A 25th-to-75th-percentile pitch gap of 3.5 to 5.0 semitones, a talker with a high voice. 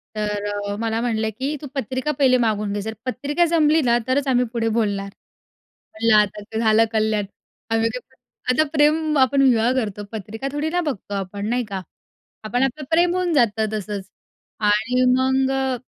Yes: average, 4.1 semitones; high, 235 Hz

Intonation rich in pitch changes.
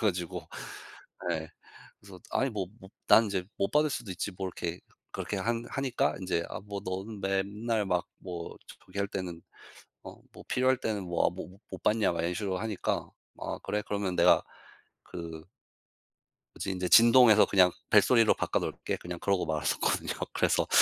No: average, 3.3 semitones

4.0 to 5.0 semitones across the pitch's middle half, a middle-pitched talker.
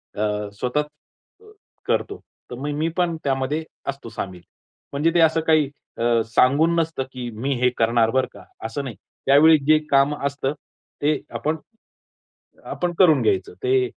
Yes: average, 4.3 semitones; medium, 145 Hz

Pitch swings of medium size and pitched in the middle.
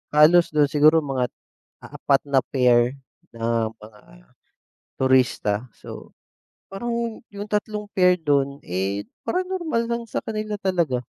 No: wide, 8.9 semitones; medium, 150 Hz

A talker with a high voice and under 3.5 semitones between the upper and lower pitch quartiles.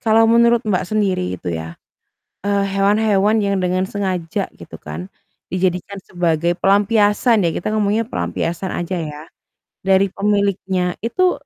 Yes: high, 195 Hz; average, 3.0 semitones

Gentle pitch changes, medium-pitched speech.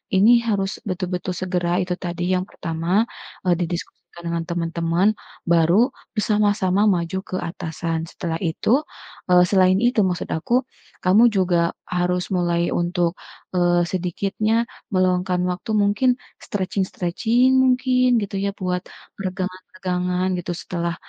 Yes: narrow, 2.1 semitones; medium, 180 Hz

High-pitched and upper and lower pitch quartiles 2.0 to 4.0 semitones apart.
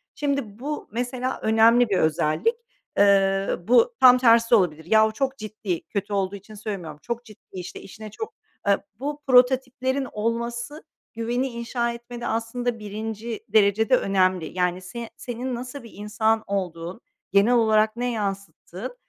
Yes: high, 225 Hz; average, 3.6 semitones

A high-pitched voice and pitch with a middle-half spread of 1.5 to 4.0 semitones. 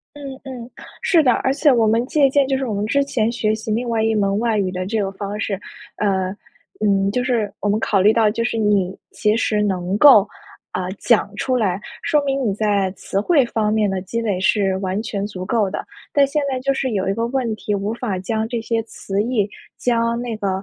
Yes: high, 220 Hz; average, 3.3 semitones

